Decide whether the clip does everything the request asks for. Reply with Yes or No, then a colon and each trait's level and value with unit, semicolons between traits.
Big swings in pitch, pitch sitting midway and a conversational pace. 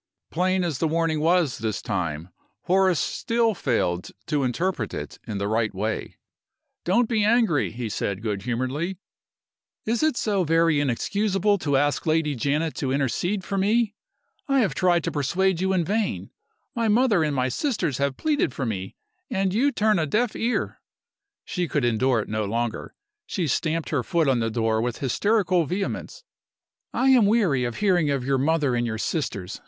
Yes: wide, 7.9 semitones; medium, 160 Hz; average, 180 wpm